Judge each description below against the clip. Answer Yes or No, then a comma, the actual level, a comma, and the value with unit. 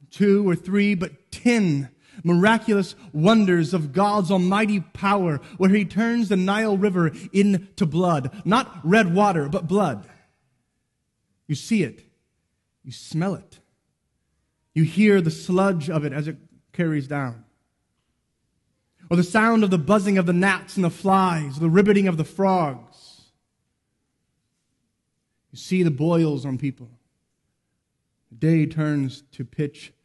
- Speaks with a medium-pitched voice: Yes, medium, 175 Hz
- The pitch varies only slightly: No, average, 5.1 semitones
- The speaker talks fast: No, slow, 135 wpm